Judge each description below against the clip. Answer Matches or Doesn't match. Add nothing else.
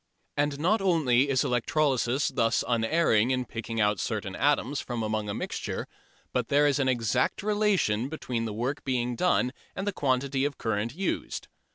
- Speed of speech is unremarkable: Matches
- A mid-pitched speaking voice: Doesn't match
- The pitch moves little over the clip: Doesn't match